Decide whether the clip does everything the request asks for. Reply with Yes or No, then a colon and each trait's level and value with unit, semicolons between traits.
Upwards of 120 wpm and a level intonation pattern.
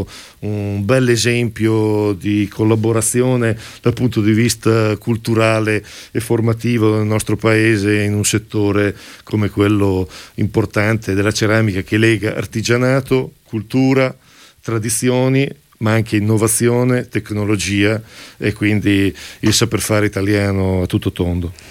No: slow, 115 wpm; narrow, 2.2 semitones